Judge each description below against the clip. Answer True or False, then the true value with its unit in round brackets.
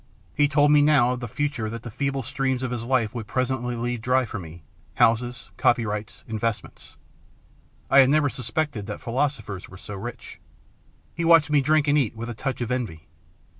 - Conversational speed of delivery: True (190 wpm)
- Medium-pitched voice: False (125 Hz)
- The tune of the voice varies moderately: True (3.7 semitones)